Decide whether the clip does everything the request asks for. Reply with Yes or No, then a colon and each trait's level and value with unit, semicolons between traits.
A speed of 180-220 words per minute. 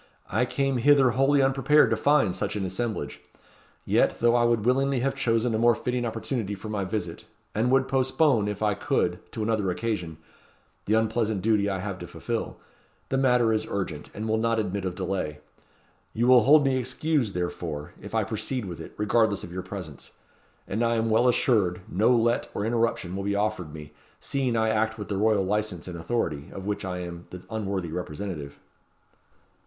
Yes: average, 190 wpm